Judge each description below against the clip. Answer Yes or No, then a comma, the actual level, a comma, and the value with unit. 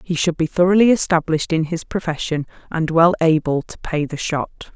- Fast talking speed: No, average, 190 wpm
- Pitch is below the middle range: No, medium, 165 Hz